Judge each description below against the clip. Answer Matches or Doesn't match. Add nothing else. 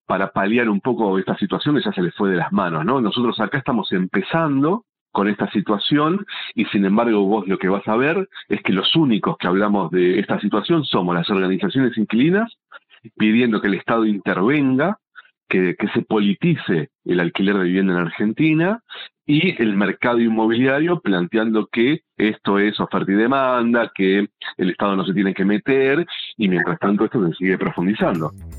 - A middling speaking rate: Matches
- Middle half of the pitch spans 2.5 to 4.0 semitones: Doesn't match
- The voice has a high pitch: Doesn't match